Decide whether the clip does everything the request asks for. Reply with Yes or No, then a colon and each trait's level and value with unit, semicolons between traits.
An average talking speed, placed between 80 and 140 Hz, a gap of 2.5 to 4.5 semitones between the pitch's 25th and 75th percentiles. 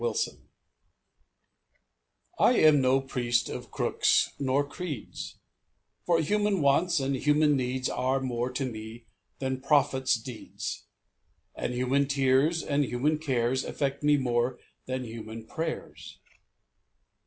No: slow, 120 wpm; low, 135 Hz; average, 2.9 semitones